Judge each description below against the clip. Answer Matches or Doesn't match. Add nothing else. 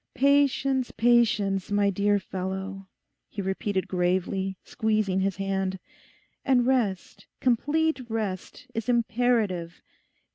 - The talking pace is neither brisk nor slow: Doesn't match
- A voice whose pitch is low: Doesn't match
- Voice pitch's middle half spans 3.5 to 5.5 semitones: Matches